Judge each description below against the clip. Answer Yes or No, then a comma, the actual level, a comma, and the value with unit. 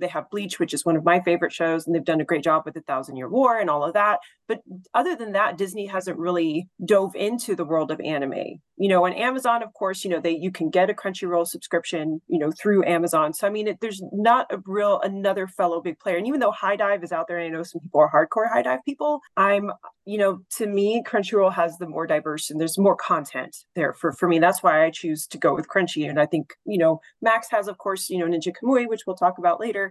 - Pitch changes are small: No, average, 3.7 semitones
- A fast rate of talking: Yes, fast, 265 wpm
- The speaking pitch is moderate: Yes, medium, 180 Hz